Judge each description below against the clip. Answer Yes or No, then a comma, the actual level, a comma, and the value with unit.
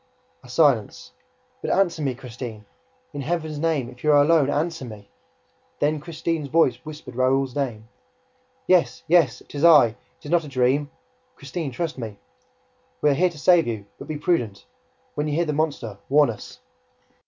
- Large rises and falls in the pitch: No, average, 4.3 semitones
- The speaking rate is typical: Yes, average, 175 wpm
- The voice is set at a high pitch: No, medium, 145 Hz